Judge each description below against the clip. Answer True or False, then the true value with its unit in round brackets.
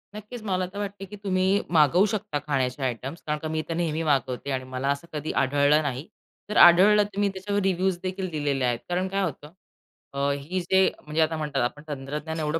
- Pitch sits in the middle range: True (160 Hz)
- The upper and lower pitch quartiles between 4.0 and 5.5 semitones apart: True (4.9 semitones)